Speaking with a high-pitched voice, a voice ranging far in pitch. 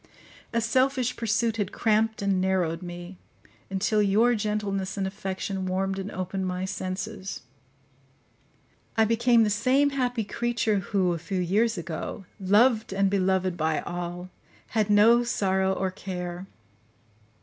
No: high, 195 Hz; average, 3.1 semitones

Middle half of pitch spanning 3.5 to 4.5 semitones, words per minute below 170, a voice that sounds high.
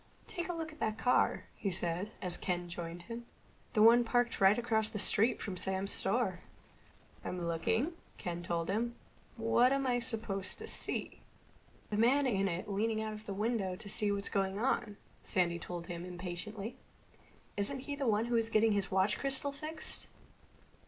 No: average, 4.1 semitones; average, 180 wpm; high, 210 Hz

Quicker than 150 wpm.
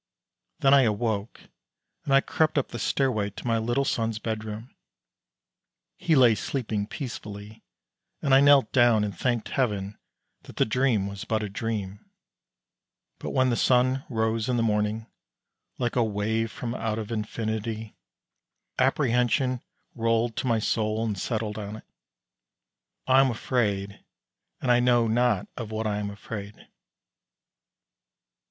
No: average, 145 wpm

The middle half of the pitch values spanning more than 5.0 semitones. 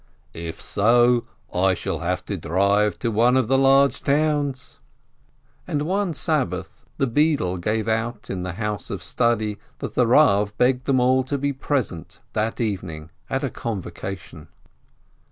Yes: wide, 5.4 semitones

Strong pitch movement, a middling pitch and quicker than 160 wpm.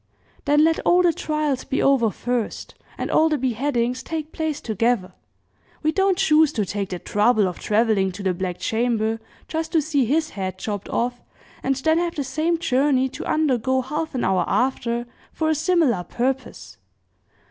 No: wide, 5.8 semitones; very high, 260 Hz; average, 175 wpm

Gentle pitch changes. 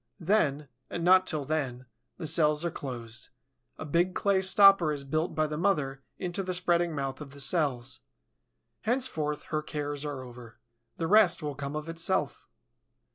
No: average, 3.9 semitones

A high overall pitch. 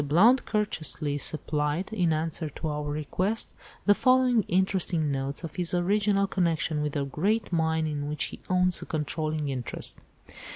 No: medium, 160 Hz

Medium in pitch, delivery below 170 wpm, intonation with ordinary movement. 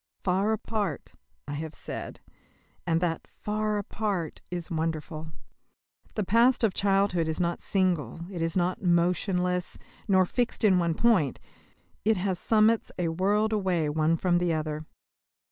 Yes: medium, 180 Hz; average, 140 wpm; average, 3.8 semitones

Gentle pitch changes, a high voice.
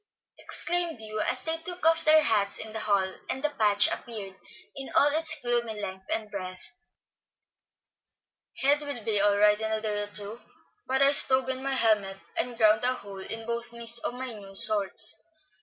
No: average, 4.2 semitones; high, 225 Hz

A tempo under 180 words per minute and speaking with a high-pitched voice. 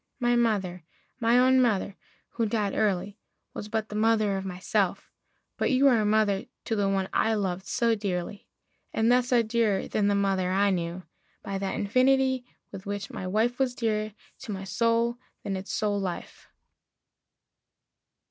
Yes: average, 165 wpm; high, 210 Hz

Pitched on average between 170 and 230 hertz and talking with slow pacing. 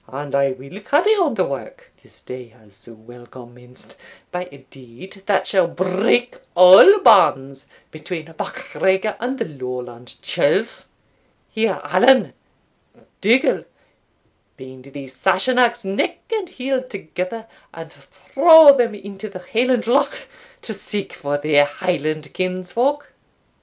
Yes: medium, 185 Hz; slow, 125 wpm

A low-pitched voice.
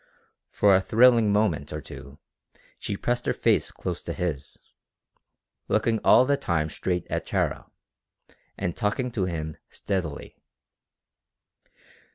Yes: very low, 95 Hz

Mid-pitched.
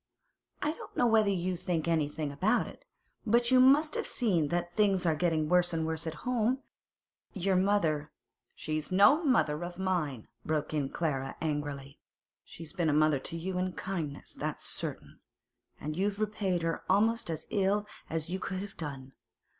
Yes: medium, 175 Hz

